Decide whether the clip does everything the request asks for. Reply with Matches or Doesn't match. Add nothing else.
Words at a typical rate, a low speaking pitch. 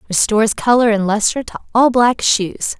Doesn't match